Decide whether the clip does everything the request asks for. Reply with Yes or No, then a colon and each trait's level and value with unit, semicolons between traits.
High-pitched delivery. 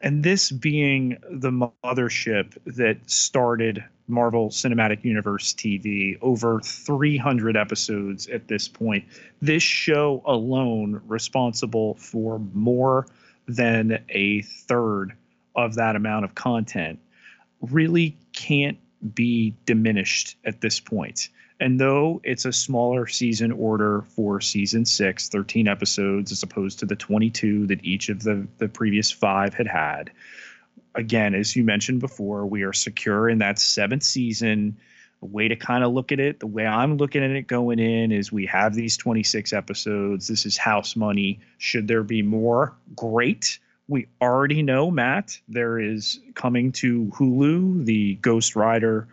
No: low, 115 Hz